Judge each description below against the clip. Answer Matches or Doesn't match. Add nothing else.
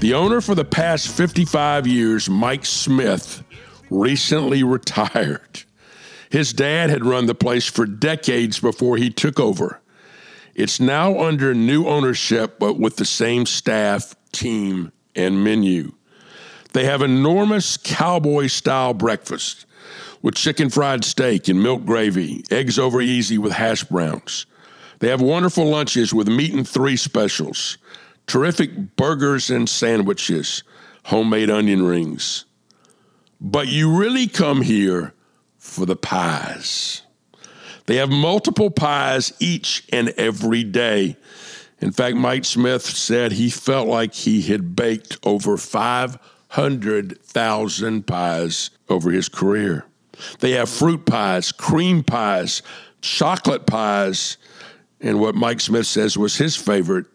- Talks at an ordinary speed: Doesn't match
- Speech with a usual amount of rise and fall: Doesn't match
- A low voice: Matches